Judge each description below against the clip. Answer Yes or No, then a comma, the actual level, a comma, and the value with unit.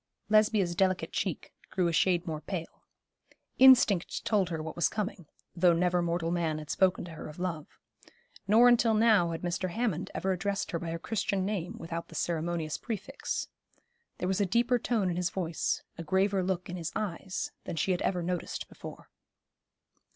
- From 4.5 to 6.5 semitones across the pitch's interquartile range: No, average, 3.0 semitones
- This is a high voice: No, medium, 180 Hz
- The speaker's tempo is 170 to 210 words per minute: Yes, average, 180 wpm